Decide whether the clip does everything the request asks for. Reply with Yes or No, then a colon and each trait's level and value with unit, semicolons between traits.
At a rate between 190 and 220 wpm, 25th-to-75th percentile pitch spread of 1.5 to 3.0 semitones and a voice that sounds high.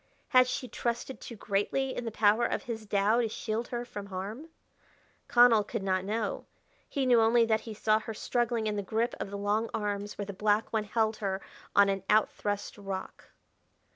Yes: average, 195 wpm; narrow, 2.5 semitones; high, 215 Hz